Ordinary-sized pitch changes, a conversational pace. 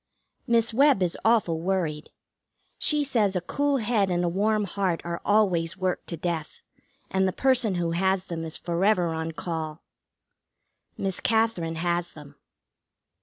Yes: average, 4.3 semitones; average, 150 wpm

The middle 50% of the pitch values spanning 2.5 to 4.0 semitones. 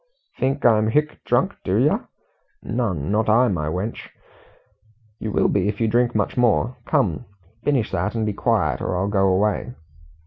Yes: average, 3.4 semitones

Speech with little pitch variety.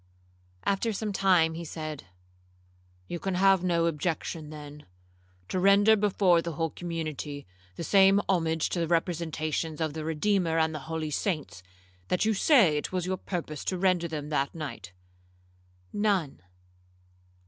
No: average, 3.7 semitones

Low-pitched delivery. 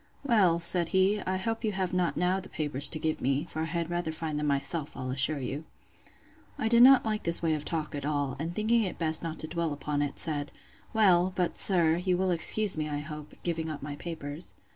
No: medium, 165 Hz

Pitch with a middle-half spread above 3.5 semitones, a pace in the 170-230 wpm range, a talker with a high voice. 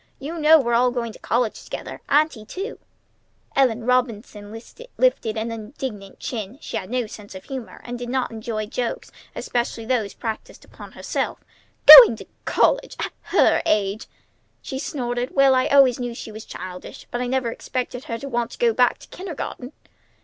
No: average, 3.1 semitones; average, 175 wpm; high, 245 Hz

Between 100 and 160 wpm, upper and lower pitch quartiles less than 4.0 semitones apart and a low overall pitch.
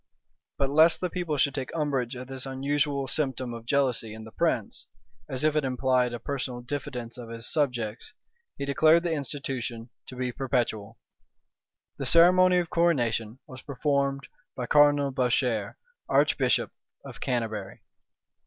Yes: average, 145 wpm; average, 3.3 semitones; low, 130 Hz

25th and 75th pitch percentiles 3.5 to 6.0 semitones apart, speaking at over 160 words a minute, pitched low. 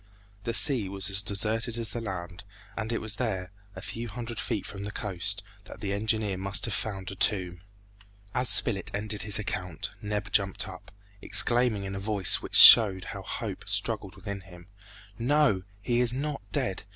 No: average, 2.9 semitones; average, 180 wpm; low, 105 Hz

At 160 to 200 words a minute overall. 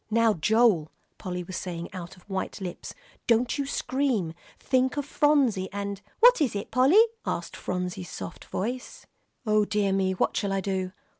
Yes: average, 170 wpm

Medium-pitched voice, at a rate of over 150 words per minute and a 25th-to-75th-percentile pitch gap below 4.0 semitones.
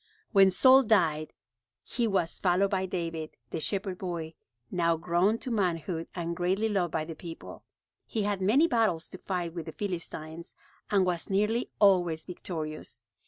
Yes: medium, 180 Hz; average, 160 wpm; average, 3.4 semitones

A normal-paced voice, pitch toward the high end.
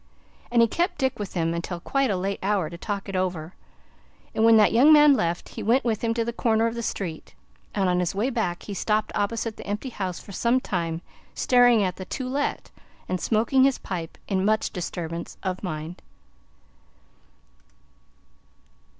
Yes: average, 185 wpm; high, 205 Hz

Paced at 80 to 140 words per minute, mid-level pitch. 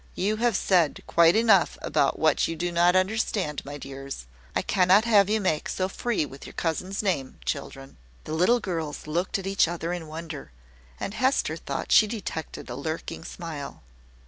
No: average, 175 wpm; medium, 175 Hz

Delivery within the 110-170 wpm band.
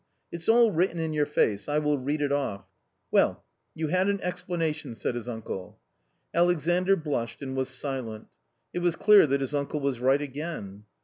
No: average, 180 wpm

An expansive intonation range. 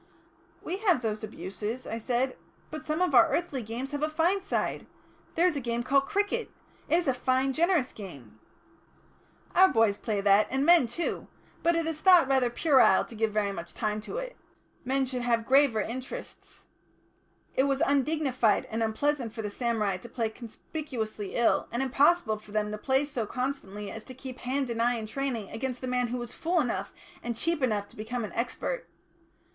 No: average, 4.7 semitones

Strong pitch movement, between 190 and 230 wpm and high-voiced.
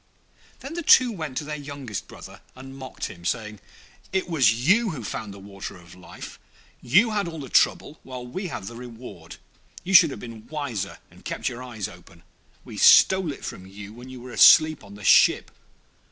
No: wide, 6.9 semitones; average, 195 wpm; low, 125 Hz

